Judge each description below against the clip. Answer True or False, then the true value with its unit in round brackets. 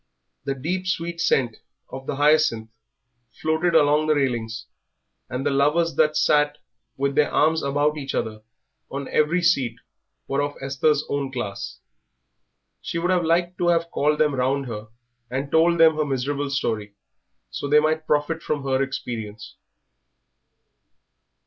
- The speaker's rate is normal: True (150 wpm)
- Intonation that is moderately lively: True (3.0 semitones)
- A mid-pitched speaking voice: True (145 Hz)